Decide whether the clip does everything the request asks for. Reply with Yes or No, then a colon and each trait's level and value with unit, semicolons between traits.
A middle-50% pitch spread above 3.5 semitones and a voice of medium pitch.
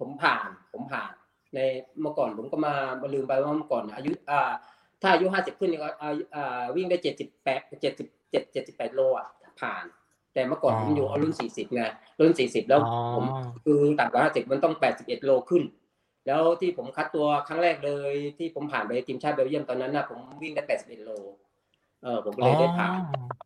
Yes: average, 4.0 semitones; medium, 145 Hz